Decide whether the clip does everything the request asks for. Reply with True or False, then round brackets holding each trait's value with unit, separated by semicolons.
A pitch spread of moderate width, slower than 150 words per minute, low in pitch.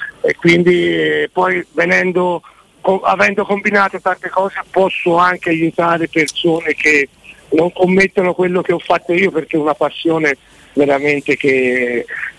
False (3.3 semitones; 135 wpm; 175 Hz)